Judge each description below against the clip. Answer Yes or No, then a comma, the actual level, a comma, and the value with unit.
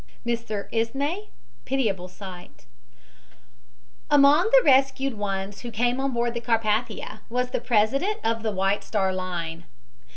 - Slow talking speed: Yes, slow, 130 wpm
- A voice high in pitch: Yes, high, 230 Hz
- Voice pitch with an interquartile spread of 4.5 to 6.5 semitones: Yes, average, 5.0 semitones